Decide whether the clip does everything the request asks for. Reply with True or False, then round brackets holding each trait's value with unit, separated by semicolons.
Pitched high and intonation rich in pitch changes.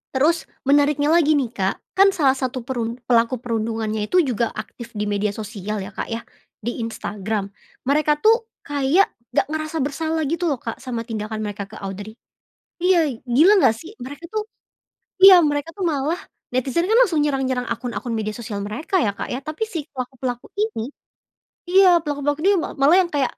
True (270 Hz; 5.9 semitones)